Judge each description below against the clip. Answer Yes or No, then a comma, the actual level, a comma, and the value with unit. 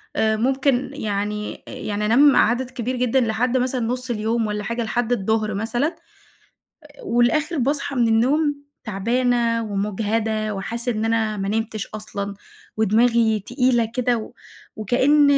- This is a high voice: Yes, high, 230 Hz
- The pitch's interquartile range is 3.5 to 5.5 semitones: No, average, 2.7 semitones